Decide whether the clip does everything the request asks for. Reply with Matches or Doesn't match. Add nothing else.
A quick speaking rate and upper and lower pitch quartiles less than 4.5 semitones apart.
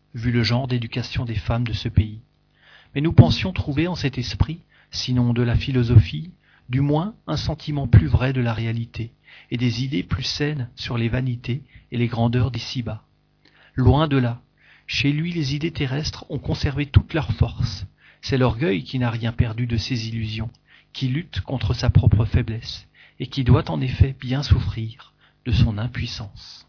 Doesn't match